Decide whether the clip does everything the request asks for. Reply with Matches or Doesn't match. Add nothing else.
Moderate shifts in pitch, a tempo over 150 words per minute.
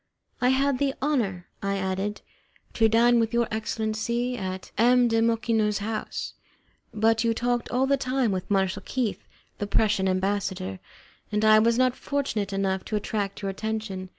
Matches